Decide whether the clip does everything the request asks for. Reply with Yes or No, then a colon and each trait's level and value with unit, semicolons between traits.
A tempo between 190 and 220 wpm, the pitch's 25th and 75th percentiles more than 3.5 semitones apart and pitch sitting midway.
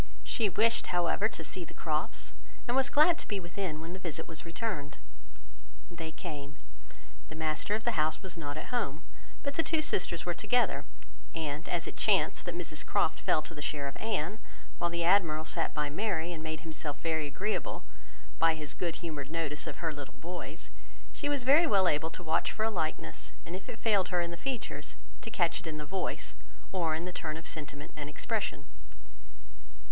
Yes: average, 200 wpm; average, 4.3 semitones; medium, 165 Hz